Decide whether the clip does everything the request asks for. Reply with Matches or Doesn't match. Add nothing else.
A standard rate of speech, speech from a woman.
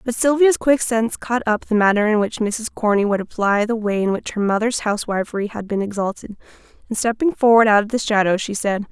Doesn't match